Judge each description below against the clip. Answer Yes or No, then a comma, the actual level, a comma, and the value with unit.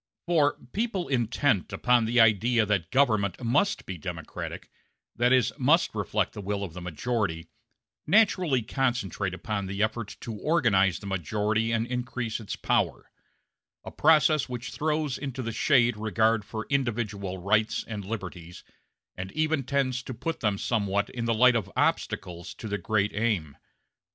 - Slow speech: No, average, 155 wpm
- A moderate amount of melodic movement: Yes, average, 4.2 semitones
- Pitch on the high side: No, low, 115 Hz